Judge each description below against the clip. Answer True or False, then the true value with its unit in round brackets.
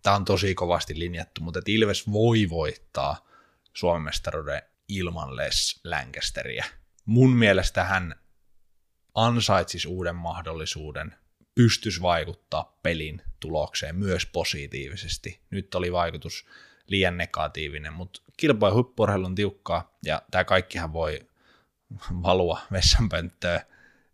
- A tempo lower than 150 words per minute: True (105 wpm)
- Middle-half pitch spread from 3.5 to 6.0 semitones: False (3.1 semitones)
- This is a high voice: False (90 Hz)